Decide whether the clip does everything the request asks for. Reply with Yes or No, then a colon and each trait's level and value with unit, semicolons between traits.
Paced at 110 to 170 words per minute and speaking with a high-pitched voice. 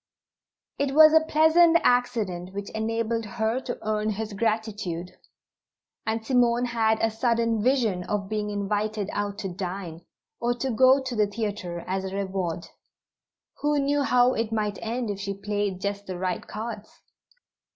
Yes: average, 150 wpm; high, 215 Hz